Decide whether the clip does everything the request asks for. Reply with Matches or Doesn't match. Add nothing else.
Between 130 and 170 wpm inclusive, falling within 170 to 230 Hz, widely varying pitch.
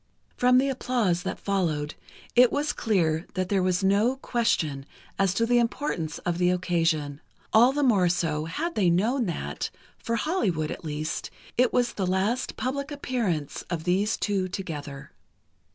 Matches